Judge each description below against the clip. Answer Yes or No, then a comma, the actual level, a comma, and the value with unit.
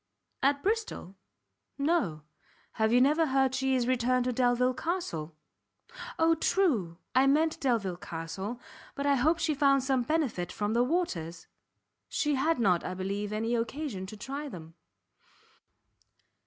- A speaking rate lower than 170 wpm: Yes, average, 140 wpm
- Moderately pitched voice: No, very high, 255 Hz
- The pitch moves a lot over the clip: Yes, wide, 6.2 semitones